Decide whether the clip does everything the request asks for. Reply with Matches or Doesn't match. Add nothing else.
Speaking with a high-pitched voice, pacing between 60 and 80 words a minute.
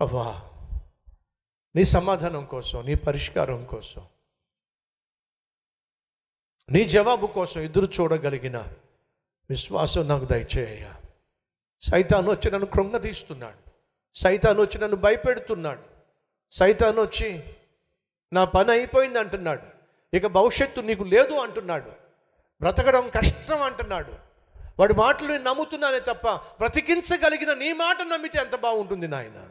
Doesn't match